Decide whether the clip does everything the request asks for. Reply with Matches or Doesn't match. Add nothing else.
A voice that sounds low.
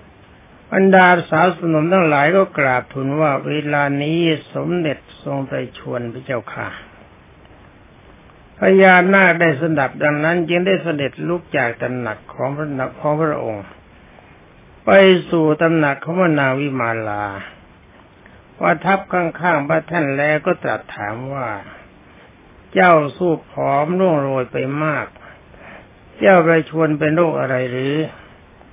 Doesn't match